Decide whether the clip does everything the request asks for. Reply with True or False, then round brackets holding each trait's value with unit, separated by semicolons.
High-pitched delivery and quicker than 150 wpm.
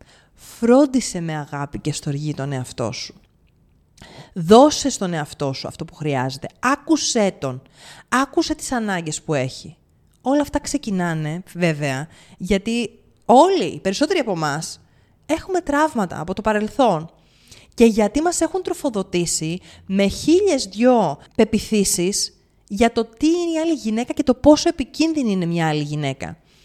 False (200 Hz; 135 wpm)